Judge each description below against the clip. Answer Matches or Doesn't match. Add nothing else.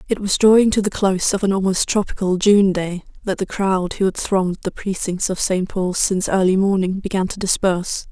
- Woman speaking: Matches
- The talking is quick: Matches